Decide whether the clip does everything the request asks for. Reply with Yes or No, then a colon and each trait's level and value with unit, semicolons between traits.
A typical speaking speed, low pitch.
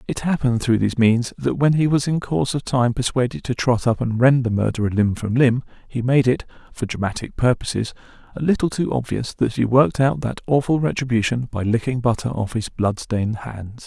No: fast, 210 wpm; low, 120 Hz